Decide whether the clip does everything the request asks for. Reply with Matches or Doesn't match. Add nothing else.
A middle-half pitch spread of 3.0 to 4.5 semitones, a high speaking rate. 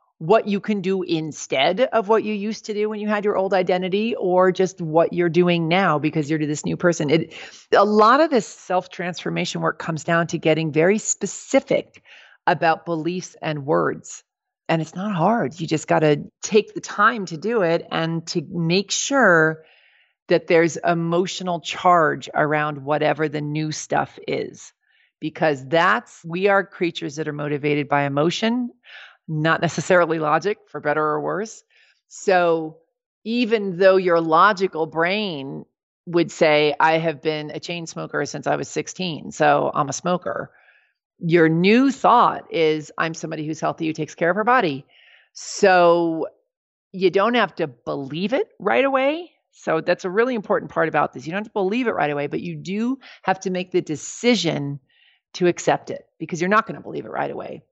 Doesn't match